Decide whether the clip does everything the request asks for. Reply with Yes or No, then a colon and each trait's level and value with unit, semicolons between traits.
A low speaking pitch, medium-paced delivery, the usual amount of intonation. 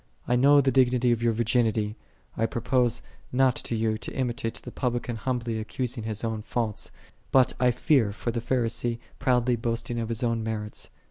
No: low, 120 Hz; average, 185 wpm; narrow, 1.8 semitones